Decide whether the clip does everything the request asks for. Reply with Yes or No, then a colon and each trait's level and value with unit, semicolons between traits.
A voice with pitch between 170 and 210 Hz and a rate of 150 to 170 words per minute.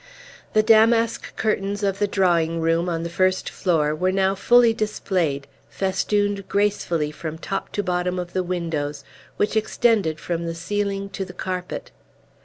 Yes: medium, 185 Hz; average, 155 wpm